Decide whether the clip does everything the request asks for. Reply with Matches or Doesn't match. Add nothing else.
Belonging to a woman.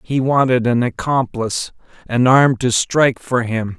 Doesn't match